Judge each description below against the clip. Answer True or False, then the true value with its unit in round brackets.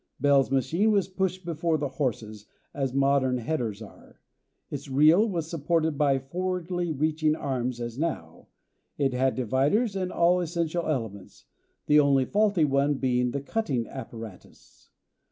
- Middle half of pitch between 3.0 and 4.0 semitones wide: False (4.7 semitones)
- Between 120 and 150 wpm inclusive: True (140 wpm)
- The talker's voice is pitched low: False (145 Hz)